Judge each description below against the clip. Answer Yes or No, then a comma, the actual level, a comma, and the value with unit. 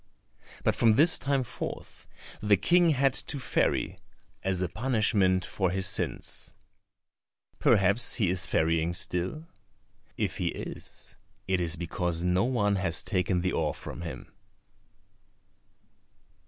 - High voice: No, very low, 95 Hz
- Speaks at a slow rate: Yes, slow, 130 wpm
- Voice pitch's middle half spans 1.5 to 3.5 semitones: No, average, 4.7 semitones